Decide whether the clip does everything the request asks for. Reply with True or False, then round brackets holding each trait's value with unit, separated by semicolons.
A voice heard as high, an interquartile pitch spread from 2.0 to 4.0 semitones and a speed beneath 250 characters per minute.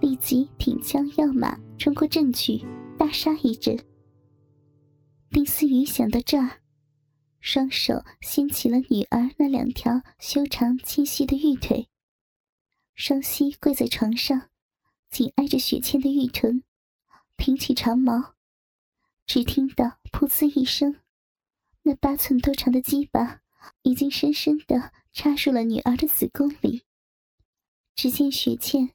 True (270 Hz; 2.6 semitones; 185 characters per minute)